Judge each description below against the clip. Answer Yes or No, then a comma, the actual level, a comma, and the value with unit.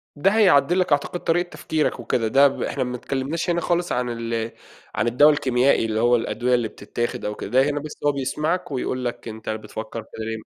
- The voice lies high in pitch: No, low, 130 Hz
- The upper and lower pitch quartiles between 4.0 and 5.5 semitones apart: Yes, average, 4.5 semitones